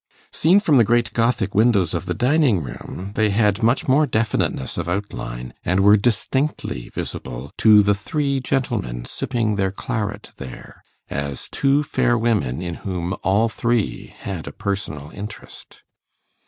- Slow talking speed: No, average, 150 wpm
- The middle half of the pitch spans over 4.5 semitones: Yes, average, 5.1 semitones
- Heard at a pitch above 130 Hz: No, low, 105 Hz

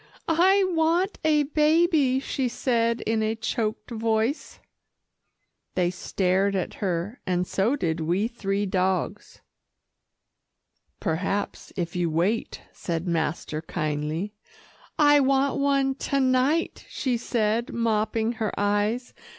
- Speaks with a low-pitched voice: No, high, 225 Hz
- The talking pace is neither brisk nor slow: No, slow, 115 wpm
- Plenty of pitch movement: Yes, wide, 6.5 semitones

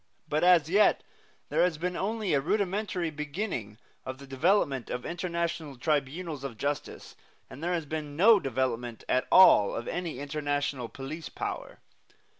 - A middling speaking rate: Yes, average, 150 wpm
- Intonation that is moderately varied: Yes, average, 4.7 semitones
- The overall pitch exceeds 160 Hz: No, medium, 150 Hz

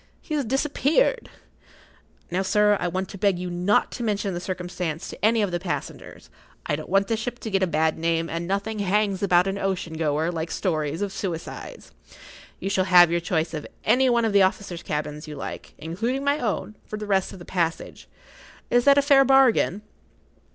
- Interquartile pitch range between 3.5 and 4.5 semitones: Yes, average, 4.1 semitones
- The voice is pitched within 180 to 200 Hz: Yes, high, 190 Hz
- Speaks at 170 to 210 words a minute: Yes, fast, 205 wpm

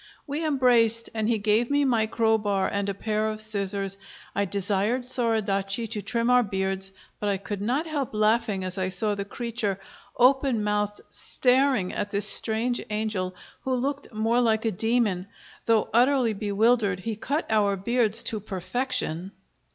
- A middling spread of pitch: Yes, average, 3.2 semitones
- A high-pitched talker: Yes, high, 220 Hz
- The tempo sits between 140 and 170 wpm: Yes, average, 160 wpm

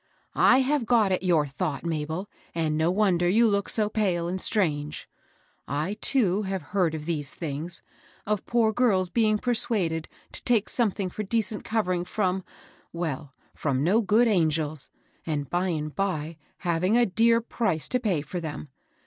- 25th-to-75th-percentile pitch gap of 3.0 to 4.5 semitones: No, average, 5.1 semitones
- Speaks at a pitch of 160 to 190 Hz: Yes, medium, 185 Hz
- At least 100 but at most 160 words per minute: No, average, 180 wpm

